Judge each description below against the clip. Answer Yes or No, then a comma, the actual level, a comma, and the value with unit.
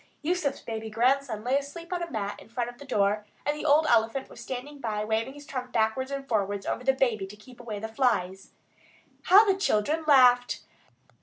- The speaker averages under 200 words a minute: No, fast, 205 wpm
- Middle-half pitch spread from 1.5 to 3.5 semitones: No, average, 4.3 semitones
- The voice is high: Yes, high, 245 Hz